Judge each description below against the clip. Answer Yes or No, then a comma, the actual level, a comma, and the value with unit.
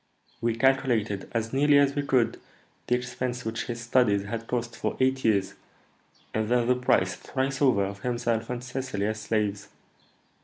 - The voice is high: No, low, 120 Hz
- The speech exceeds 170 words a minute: No, average, 165 wpm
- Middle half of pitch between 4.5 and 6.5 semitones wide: No, average, 3.0 semitones